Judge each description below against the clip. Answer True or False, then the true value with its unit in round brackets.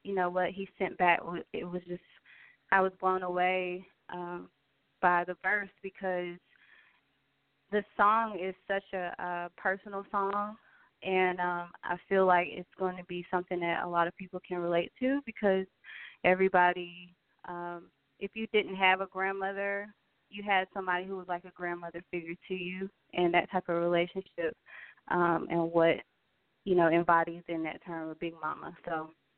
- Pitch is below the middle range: False (180 Hz)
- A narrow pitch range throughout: True (1.7 semitones)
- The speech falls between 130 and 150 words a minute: False (165 wpm)